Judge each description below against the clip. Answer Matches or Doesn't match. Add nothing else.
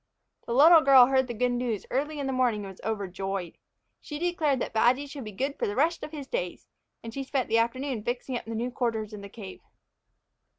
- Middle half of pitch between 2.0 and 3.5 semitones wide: Doesn't match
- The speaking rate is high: Matches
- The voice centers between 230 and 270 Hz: Matches